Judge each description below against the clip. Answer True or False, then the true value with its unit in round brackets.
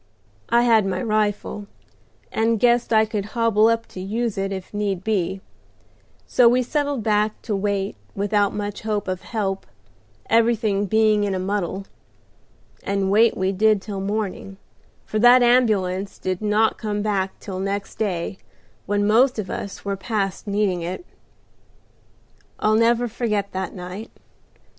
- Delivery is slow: False (150 wpm)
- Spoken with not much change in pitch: True (2.3 semitones)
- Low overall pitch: False (210 Hz)